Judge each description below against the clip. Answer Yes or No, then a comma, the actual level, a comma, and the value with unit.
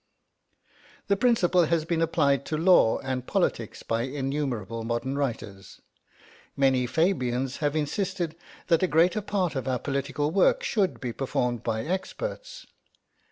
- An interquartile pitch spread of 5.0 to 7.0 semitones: Yes, wide, 5.6 semitones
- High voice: No, medium, 145 Hz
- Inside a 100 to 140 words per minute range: Yes, slow, 135 wpm